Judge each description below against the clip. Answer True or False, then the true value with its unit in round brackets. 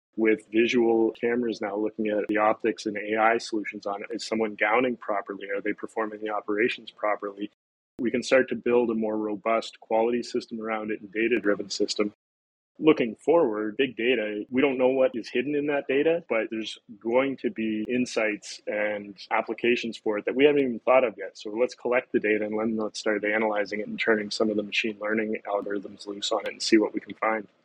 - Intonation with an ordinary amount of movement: False (2.3 semitones)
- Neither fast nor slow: False (210 wpm)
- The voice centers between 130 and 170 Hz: False (110 Hz)